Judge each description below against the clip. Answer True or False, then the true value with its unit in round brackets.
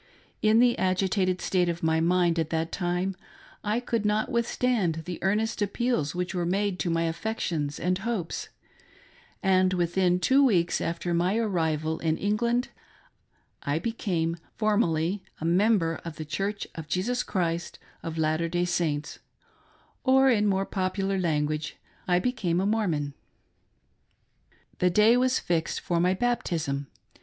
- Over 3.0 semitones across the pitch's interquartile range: True (4.1 semitones)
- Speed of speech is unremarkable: True (150 wpm)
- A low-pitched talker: False (180 Hz)